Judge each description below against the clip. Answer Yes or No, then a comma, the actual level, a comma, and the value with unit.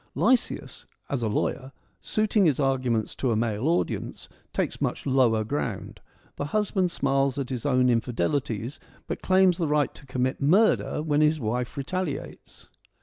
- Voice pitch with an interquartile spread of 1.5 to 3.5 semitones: No, average, 4.2 semitones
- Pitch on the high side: No, low, 135 Hz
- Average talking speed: Yes, average, 150 wpm